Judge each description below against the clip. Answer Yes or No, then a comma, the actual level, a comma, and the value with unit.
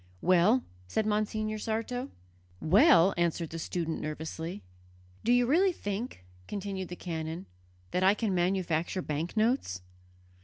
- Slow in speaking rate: Yes, slow, 120 wpm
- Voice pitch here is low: No, high, 190 Hz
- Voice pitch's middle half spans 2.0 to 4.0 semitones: No, average, 4.8 semitones